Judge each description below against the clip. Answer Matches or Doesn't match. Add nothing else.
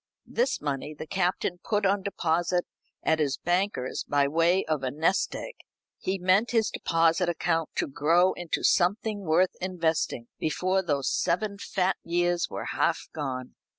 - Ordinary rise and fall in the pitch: Matches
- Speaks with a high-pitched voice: Doesn't match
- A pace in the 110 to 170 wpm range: Matches